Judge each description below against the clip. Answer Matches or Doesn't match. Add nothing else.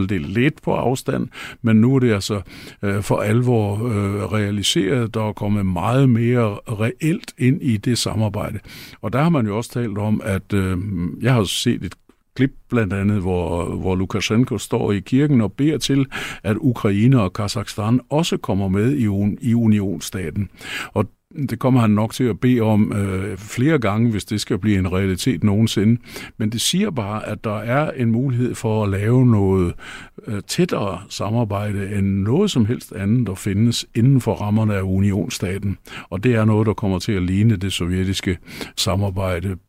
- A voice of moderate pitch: Doesn't match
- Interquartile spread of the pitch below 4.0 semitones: Matches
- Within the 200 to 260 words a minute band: Doesn't match